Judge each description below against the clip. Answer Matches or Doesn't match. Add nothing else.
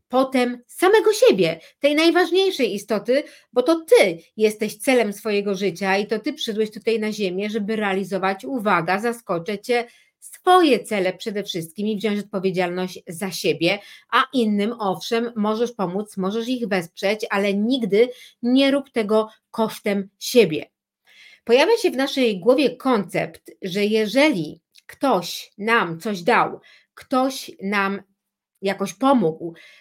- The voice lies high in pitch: Matches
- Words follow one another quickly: Doesn't match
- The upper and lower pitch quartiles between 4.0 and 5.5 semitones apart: Matches